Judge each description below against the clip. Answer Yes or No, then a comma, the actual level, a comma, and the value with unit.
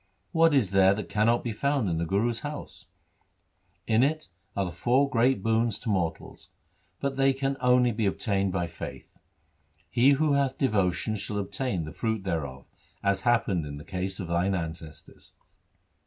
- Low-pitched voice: Yes, low, 105 Hz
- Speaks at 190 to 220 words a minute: No, average, 170 wpm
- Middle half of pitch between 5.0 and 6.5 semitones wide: Yes, wide, 5.5 semitones